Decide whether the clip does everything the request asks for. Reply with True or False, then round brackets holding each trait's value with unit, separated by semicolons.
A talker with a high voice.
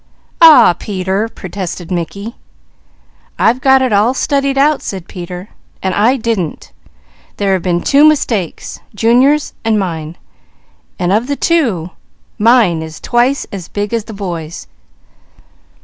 True (205 Hz)